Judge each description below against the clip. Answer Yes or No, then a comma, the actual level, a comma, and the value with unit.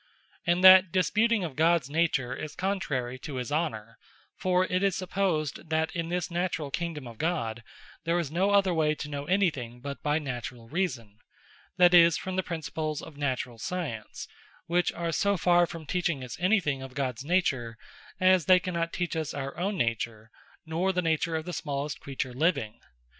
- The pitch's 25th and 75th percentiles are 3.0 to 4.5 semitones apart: No, average, 4.9 semitones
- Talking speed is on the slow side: No, average, 185 wpm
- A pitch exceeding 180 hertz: No, medium, 160 Hz